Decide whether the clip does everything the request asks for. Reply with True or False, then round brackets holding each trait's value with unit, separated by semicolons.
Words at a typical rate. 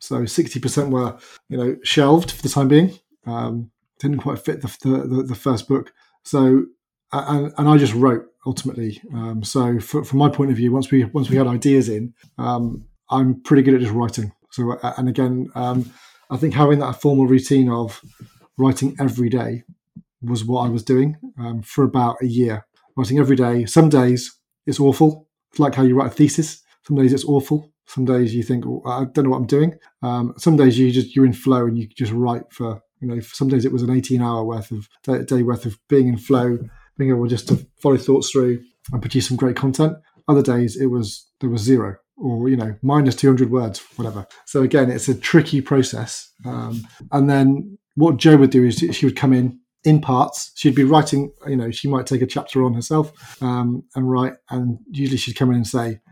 False (215 wpm)